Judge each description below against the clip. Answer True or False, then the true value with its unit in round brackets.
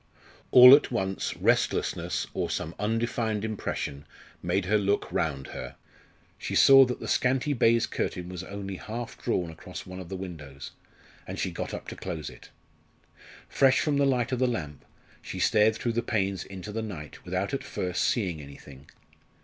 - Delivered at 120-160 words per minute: False (175 wpm)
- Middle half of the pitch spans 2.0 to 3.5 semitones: False (5.0 semitones)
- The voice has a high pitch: False (100 Hz)